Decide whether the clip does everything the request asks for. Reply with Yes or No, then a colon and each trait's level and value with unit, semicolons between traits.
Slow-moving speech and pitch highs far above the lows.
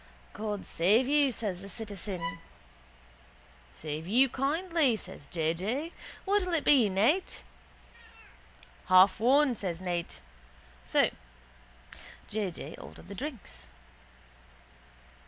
Yes: slow, 100 wpm; wide, 7.3 semitones